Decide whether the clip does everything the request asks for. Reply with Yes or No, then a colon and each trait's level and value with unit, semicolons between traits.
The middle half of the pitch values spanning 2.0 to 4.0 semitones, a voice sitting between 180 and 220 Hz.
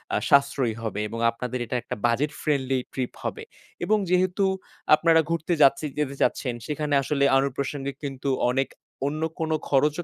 No: average, 2.8 semitones; medium, 140 Hz